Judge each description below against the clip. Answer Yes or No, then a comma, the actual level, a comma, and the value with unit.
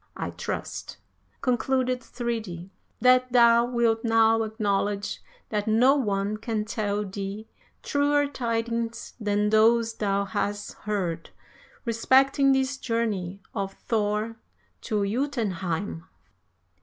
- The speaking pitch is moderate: No, high, 225 Hz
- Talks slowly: Yes, slow, 105 wpm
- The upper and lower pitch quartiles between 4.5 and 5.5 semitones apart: No, average, 2.8 semitones